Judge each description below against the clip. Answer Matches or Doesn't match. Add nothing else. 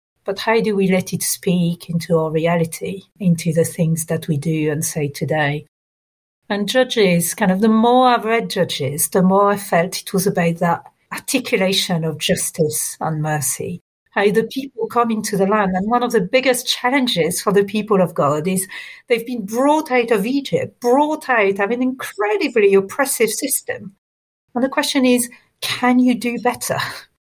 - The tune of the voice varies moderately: Doesn't match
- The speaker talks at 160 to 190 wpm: Matches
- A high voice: Matches